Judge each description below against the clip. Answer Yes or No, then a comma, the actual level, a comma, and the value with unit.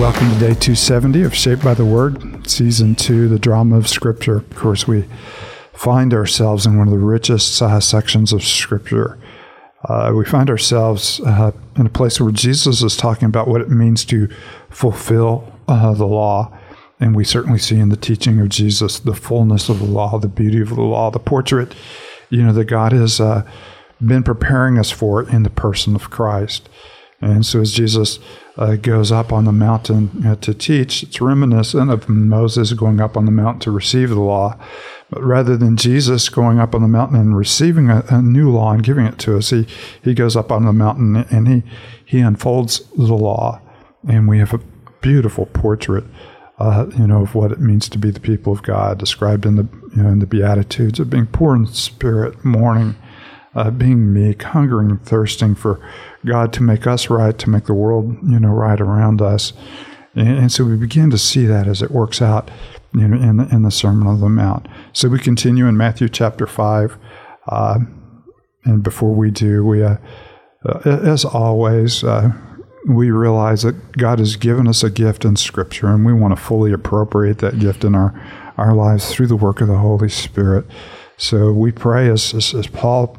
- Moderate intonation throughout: No, narrow, 2.2 semitones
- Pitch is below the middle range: Yes, low, 115 Hz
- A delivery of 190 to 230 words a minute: Yes, average, 200 wpm